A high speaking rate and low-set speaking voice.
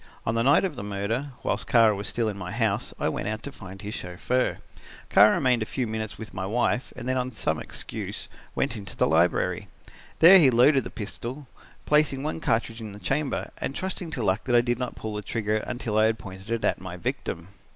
Yes: fast, 225 wpm; low, 115 Hz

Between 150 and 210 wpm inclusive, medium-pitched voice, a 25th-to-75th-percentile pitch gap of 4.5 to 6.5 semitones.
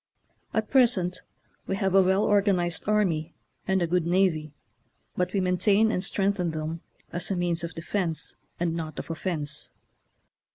No: average, 155 wpm; medium, 180 Hz; average, 2.8 semitones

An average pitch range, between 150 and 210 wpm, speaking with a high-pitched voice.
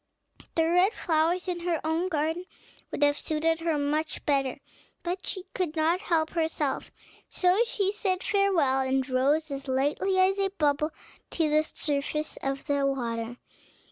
Yes: average, 4.0 semitones; average, 155 wpm; very high, 315 Hz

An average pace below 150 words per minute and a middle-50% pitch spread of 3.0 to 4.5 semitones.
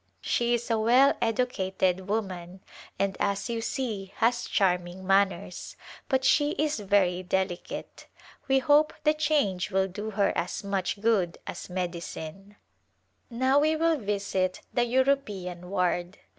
No: slow, 135 wpm; average, 5.2 semitones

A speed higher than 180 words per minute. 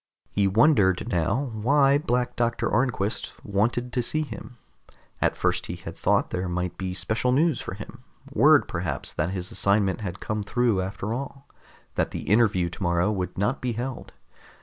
No: average, 170 wpm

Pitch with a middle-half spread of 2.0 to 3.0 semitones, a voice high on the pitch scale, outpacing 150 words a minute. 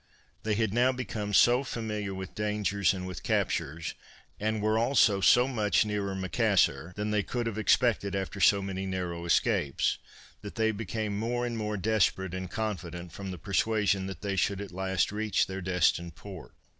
No: narrow, 2.6 semitones; low, 100 Hz; average, 175 wpm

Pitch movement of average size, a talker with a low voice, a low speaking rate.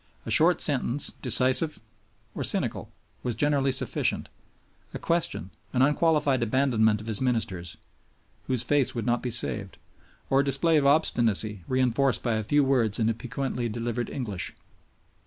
No: average, 3.6 semitones; low, 125 Hz; average, 150 wpm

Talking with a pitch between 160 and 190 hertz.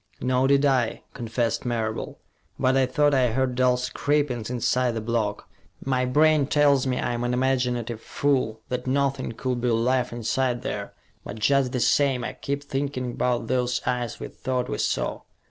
No: low, 125 Hz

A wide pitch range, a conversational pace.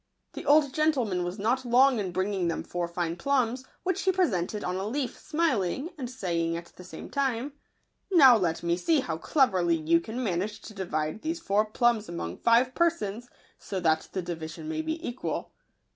Yes: wide, 7.4 semitones; average, 190 wpm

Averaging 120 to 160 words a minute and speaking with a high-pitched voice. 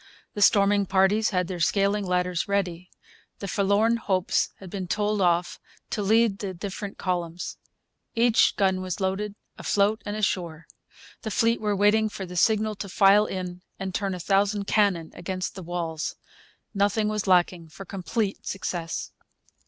Yes: average, 155 wpm; high, 195 Hz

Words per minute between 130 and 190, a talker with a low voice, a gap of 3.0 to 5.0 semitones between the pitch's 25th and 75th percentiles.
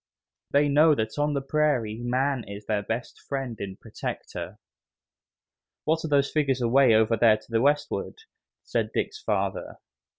Yes: average, 155 wpm; low, 130 Hz; average, 4.7 semitones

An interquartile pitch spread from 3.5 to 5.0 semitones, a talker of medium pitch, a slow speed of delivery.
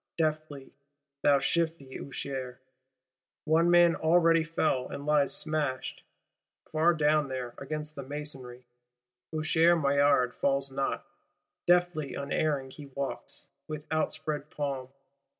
No: narrow, 2.4 semitones; medium, 150 Hz; slow, 110 wpm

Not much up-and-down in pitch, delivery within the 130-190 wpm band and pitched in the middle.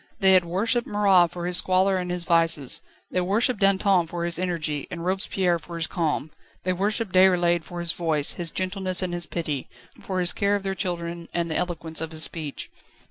No: narrow, 2.1 semitones; average, 200 wpm; medium, 175 Hz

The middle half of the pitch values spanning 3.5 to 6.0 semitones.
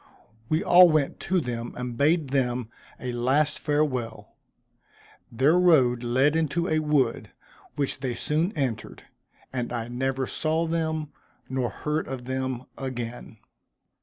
Yes: average, 4.1 semitones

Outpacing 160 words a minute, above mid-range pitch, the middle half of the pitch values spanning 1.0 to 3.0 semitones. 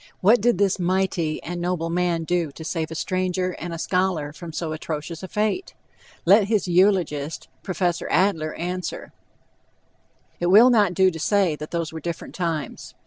No: average, 170 wpm; medium, 175 Hz; average, 2.7 semitones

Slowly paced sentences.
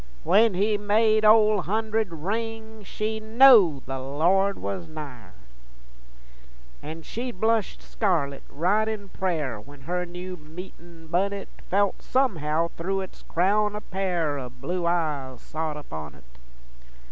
Yes: slow, 130 wpm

